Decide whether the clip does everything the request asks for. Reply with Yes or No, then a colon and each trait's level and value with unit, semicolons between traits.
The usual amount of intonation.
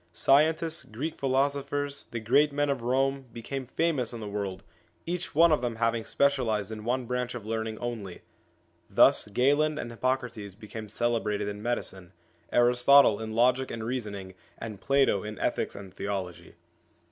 Yes: average, 4.3 semitones